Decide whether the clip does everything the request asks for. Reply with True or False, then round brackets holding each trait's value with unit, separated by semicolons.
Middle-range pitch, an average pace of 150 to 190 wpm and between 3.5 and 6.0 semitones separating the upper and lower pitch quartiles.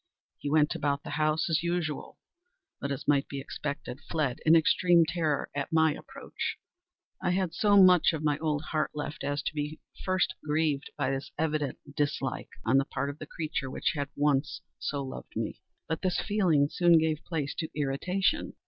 False (155 Hz; 185 wpm; 2.4 semitones)